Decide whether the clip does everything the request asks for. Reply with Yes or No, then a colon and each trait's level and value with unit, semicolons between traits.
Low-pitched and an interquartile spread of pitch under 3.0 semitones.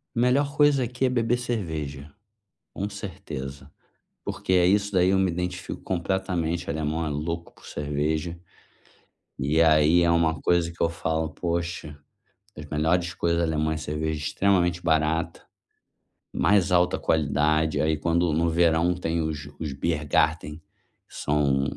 Yes: very low, 85 Hz; narrow, 2.6 semitones